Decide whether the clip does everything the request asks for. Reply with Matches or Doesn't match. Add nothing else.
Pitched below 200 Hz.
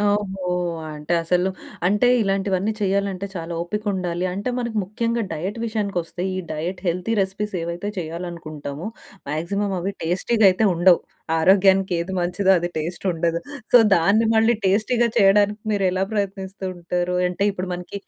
Matches